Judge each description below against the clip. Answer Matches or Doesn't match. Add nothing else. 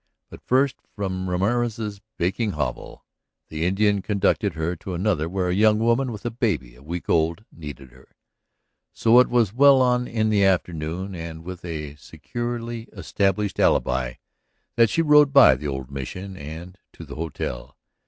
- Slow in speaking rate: Doesn't match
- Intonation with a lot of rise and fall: Matches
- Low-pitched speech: Matches